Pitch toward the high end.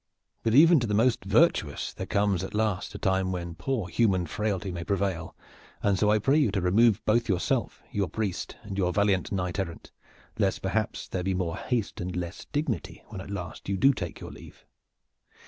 No: low, 100 Hz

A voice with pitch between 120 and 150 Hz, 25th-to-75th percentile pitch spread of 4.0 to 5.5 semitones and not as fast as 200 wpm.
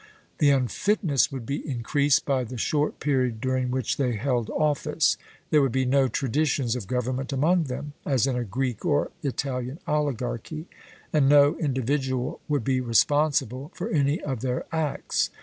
No: low, 135 Hz; narrow, 2.6 semitones; average, 160 wpm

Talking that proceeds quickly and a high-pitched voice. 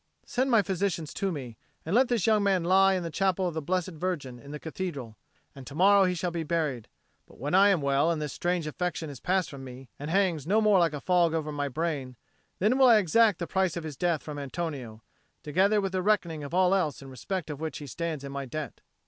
No: fast, 245 wpm; medium, 170 Hz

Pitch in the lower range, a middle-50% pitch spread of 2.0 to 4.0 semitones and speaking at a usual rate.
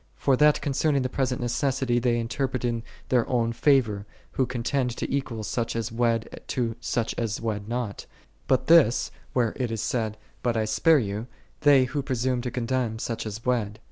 Yes: low, 120 Hz; narrow, 2.5 semitones; average, 180 wpm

